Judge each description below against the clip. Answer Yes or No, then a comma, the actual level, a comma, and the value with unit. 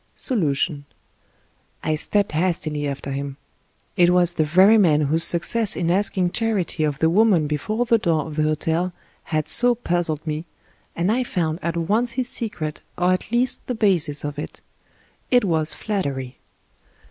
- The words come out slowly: No, average, 160 wpm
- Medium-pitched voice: Yes, medium, 170 Hz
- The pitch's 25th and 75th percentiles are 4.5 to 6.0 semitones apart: Yes, average, 5.2 semitones